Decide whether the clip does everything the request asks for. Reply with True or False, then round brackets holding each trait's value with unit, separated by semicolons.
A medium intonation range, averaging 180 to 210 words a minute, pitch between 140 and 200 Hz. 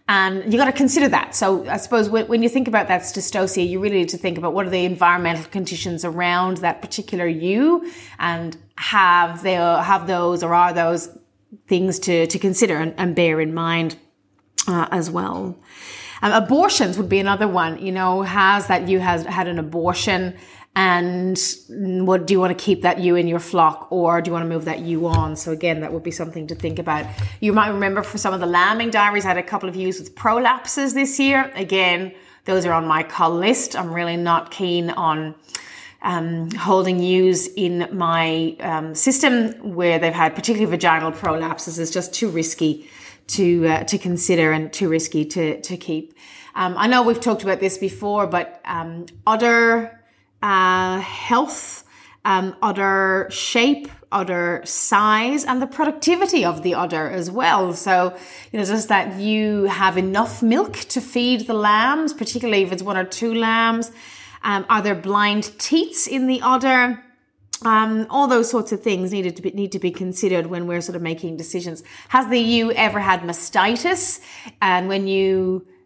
True (3.8 semitones; 185 wpm; 185 Hz)